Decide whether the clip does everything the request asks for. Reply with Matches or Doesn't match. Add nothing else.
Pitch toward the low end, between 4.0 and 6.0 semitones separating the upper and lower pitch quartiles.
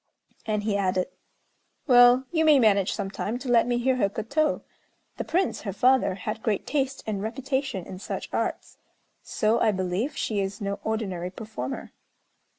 Doesn't match